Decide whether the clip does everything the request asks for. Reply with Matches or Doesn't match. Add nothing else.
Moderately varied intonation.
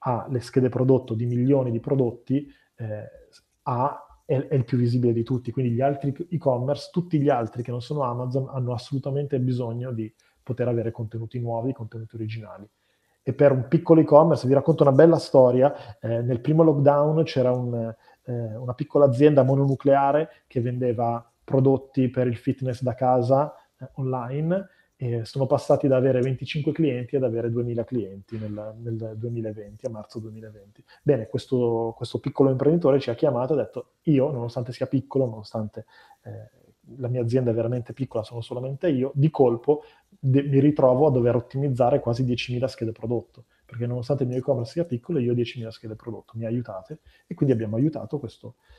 Matches